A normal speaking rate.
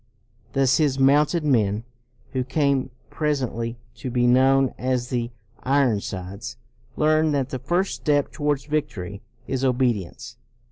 No: slow, 130 wpm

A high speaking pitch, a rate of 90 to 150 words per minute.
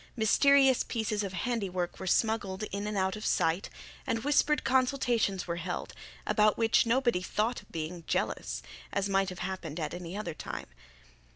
No: high, 205 Hz; average, 165 wpm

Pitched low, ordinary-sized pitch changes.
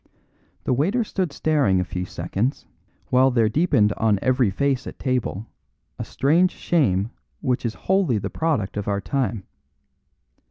No: low, 125 Hz; wide, 6.0 semitones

